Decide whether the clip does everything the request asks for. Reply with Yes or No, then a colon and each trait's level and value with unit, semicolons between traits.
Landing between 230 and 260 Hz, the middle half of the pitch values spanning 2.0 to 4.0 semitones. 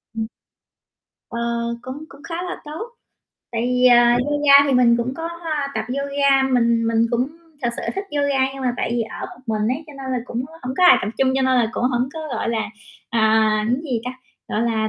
Yes: very high, 250 Hz; average, 3.2 semitones